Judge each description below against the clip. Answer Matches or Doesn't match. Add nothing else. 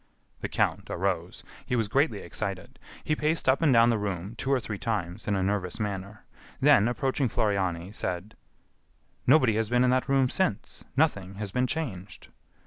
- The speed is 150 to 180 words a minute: Matches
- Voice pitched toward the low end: Matches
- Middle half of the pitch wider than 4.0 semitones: Matches